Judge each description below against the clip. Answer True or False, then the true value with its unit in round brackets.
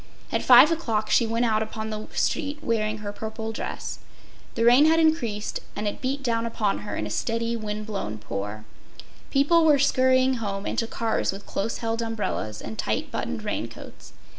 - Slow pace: False (185 wpm)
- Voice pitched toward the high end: True (225 Hz)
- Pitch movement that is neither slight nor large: True (3.5 semitones)